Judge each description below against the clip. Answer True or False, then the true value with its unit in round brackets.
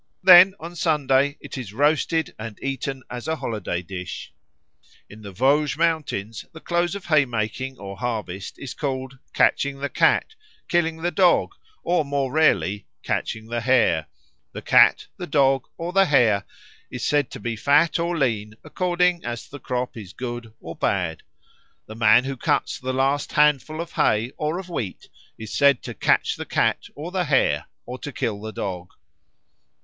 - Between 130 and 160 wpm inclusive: False (170 wpm)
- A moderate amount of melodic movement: False (6.0 semitones)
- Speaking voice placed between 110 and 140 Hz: True (135 Hz)